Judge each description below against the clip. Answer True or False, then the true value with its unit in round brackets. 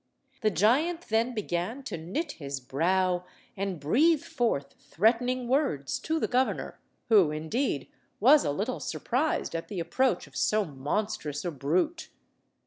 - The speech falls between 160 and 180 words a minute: False (140 wpm)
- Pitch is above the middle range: True (210 Hz)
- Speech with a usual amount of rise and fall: False (7.8 semitones)